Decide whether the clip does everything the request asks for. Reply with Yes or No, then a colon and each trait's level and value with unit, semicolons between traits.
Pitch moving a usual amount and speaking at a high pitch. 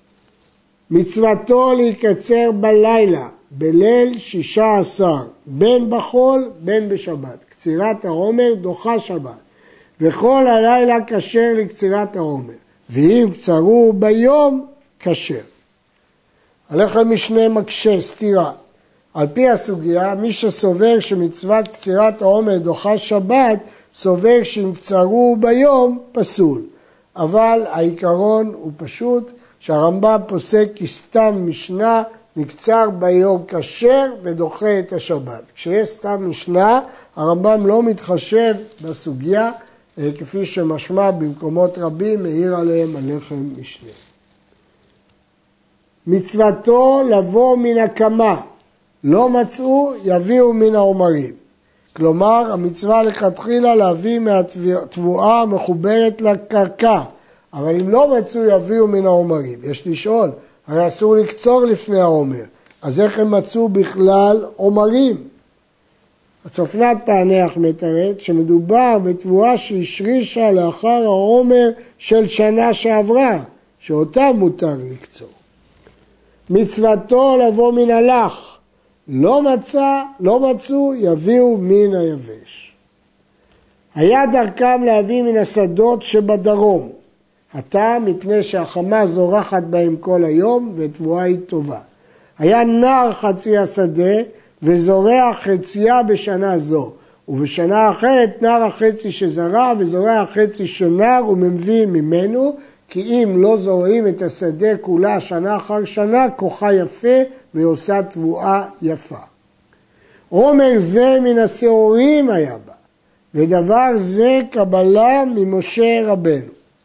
Yes: average, 4.6 semitones; high, 205 Hz